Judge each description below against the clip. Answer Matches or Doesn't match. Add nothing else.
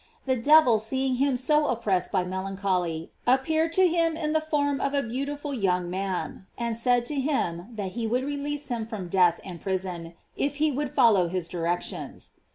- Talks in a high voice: Matches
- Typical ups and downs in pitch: Doesn't match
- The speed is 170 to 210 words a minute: Matches